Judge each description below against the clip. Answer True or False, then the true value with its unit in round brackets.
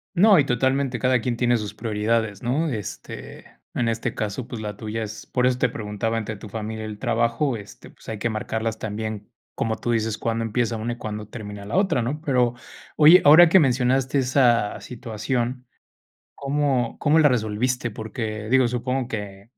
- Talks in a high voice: False (115 Hz)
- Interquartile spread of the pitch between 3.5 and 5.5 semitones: False (2.8 semitones)